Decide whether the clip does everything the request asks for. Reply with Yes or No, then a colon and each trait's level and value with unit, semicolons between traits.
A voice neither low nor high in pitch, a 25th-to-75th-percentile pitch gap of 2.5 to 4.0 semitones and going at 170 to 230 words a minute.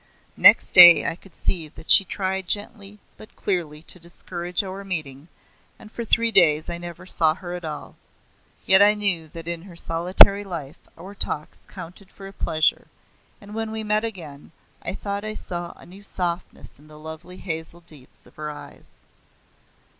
Yes: medium, 175 Hz; average, 3.5 semitones; average, 175 wpm